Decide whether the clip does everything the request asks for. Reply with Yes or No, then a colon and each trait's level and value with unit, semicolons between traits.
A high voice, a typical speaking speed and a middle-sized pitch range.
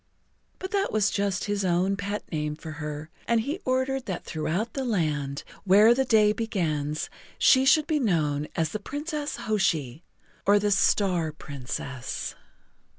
No: high, 195 Hz; average, 150 wpm; wide, 7.1 semitones